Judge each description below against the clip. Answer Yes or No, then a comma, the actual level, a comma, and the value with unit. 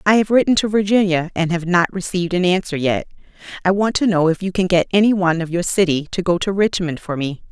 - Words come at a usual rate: No, fast, 245 wpm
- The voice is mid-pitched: Yes, medium, 180 Hz